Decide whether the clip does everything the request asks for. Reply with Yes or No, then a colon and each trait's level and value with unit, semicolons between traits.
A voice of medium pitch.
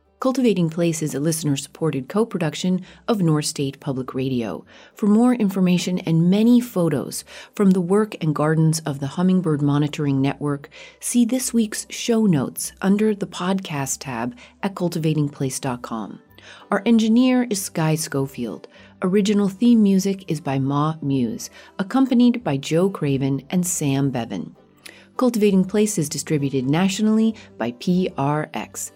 Yes: medium, 170 Hz